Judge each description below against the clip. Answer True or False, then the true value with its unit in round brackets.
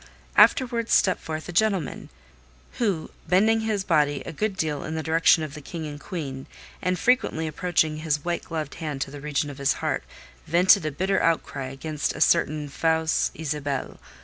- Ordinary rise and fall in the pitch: True (3.6 semitones)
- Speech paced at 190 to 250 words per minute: False (175 wpm)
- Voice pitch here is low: False (160 Hz)